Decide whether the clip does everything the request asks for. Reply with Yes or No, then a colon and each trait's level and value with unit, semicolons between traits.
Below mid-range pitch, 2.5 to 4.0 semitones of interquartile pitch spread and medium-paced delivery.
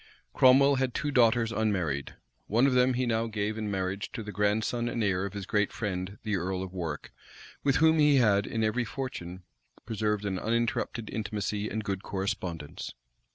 Yes: low, 105 Hz; average, 3.4 semitones; average, 180 wpm